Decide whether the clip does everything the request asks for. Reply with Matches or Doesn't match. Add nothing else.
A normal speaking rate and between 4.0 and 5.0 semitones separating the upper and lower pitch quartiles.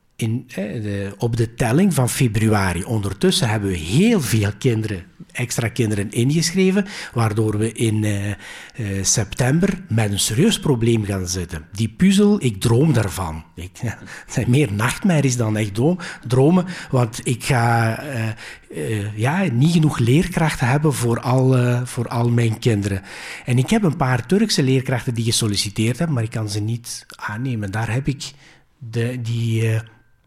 Matches